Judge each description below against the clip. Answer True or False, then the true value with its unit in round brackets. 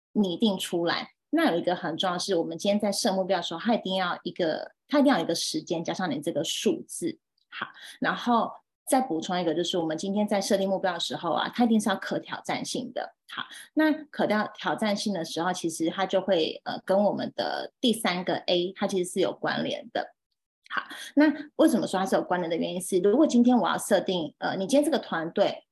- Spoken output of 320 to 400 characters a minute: True (325 characters per minute)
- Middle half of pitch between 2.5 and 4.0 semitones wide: False (4.8 semitones)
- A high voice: True (195 Hz)